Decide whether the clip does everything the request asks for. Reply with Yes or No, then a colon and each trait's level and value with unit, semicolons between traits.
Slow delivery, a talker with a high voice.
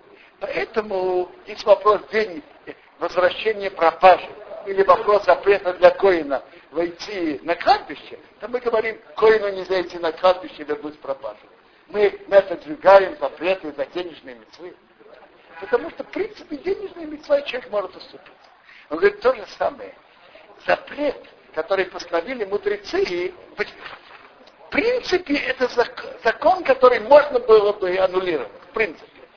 No: average, 130 wpm; high, 210 Hz